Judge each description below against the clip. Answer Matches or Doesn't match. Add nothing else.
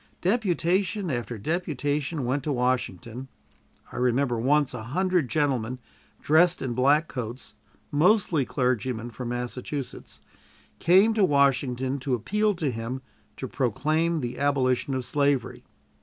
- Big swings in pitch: Doesn't match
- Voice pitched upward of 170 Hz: Doesn't match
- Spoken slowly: Matches